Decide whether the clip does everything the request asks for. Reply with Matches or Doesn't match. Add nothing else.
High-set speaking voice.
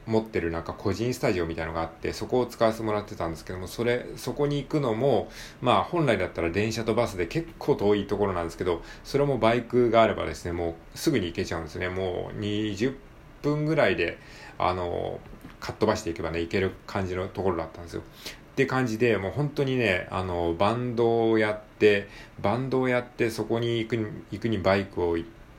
Doesn't match